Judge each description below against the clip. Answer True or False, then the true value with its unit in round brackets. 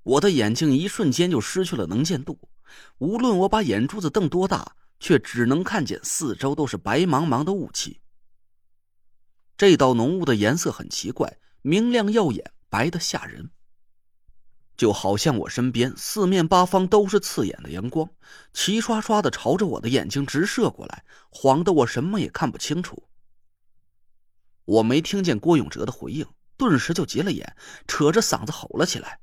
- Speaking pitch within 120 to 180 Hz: True (140 Hz)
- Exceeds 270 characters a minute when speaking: False (250 characters per minute)